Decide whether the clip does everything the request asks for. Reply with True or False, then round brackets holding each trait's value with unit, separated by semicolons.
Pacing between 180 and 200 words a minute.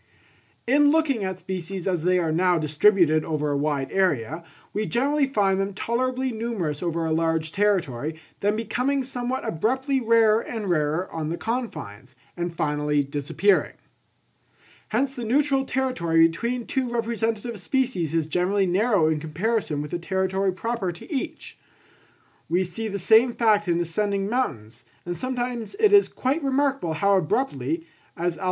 False (155 wpm)